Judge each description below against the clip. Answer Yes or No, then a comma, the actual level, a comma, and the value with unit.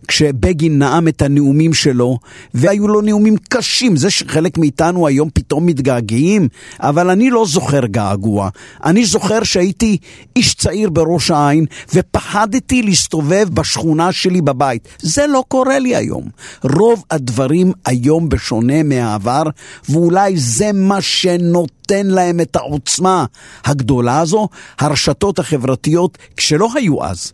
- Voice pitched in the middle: Yes, medium, 165 Hz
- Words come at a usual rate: Yes, average, 125 wpm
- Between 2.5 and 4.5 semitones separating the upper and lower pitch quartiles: No, wide, 5.5 semitones